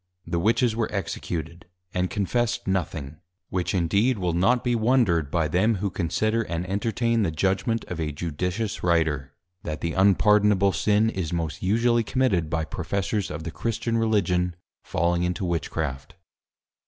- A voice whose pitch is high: No, very low, 95 Hz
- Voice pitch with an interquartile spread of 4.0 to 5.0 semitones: Yes, average, 4.7 semitones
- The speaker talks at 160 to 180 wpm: No, average, 150 wpm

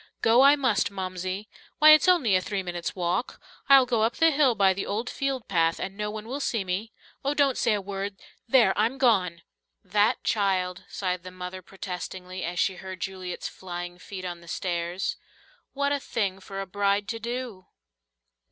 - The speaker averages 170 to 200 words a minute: Yes, average, 190 wpm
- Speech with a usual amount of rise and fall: Yes, average, 4.2 semitones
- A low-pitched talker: No, high, 200 Hz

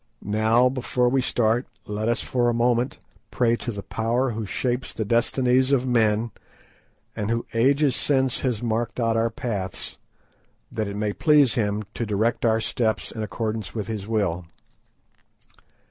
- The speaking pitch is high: No, low, 115 Hz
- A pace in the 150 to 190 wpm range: Yes, average, 160 wpm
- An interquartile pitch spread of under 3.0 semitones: Yes, narrow, 2.4 semitones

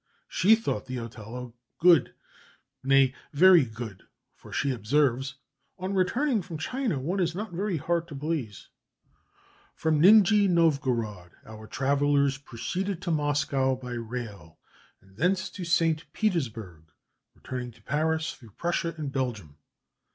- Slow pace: Yes, slow, 130 wpm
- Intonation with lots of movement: Yes, wide, 6.2 semitones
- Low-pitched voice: No, medium, 145 Hz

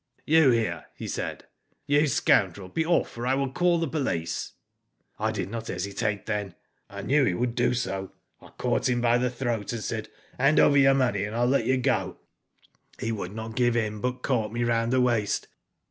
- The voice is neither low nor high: No, low, 120 Hz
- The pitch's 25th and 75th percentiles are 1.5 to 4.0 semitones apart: Yes, average, 3.3 semitones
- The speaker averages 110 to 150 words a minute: No, fast, 205 wpm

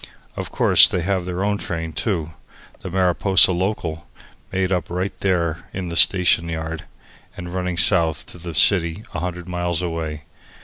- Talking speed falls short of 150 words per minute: No, average, 165 wpm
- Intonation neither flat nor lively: No, narrow, 2.0 semitones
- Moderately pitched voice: No, very low, 90 Hz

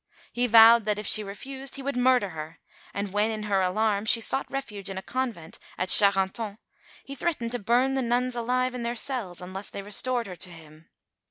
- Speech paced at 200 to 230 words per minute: Yes, fast, 205 wpm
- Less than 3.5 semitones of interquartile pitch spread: No, average, 4.2 semitones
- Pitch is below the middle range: No, high, 220 Hz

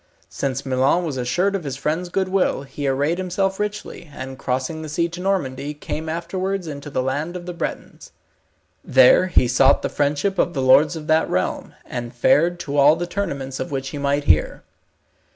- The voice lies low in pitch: No, medium, 150 Hz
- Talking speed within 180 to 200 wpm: Yes, average, 190 wpm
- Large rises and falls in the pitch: No, average, 4.7 semitones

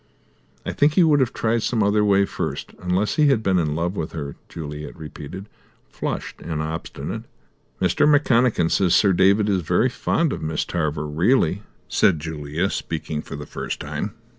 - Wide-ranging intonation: Yes, wide, 5.7 semitones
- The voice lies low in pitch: Yes, very low, 90 Hz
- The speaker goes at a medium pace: Yes, average, 175 wpm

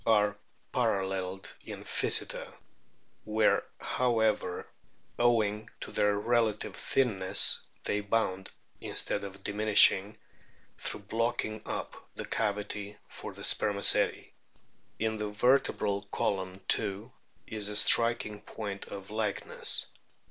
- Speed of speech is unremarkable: No, slow, 105 wpm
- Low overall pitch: Yes, low, 105 Hz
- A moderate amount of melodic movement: No, narrow, 1.8 semitones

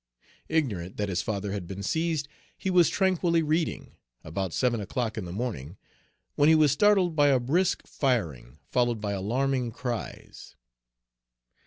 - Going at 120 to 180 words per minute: Yes, average, 150 wpm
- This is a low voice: Yes, low, 125 Hz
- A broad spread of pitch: Yes, wide, 7.7 semitones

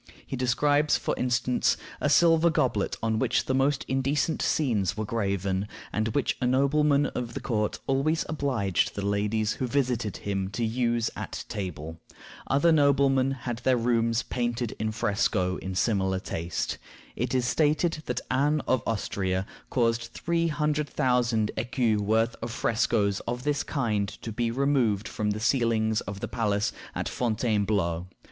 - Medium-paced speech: Yes, average, 155 wpm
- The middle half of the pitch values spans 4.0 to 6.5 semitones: Yes, average, 4.3 semitones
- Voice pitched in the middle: No, low, 120 Hz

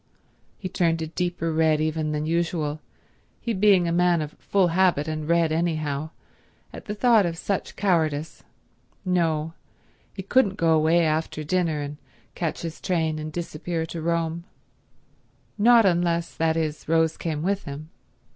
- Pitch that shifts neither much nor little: No, narrow, 2.3 semitones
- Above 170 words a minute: No, average, 155 wpm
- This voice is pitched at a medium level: Yes, medium, 165 Hz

